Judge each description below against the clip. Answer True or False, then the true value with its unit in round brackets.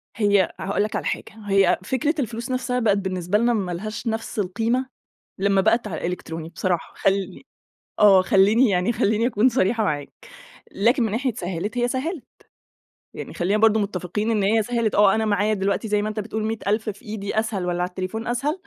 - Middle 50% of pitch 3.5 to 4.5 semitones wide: False (3.0 semitones)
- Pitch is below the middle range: False (210 Hz)